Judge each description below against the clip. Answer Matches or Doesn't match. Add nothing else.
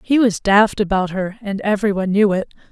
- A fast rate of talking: Matches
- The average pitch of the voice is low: Doesn't match